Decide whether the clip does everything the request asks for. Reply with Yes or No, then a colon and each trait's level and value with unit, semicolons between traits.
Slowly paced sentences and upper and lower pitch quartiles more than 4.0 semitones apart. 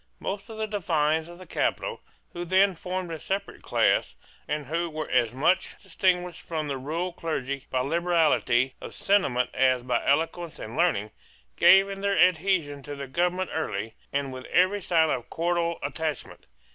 No: average, 170 wpm; average, 4.6 semitones